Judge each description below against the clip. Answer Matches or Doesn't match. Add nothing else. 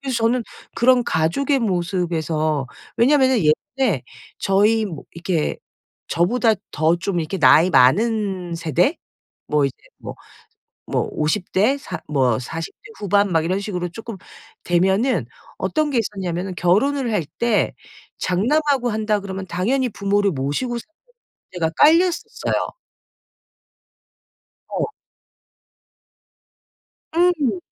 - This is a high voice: Matches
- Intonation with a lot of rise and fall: Matches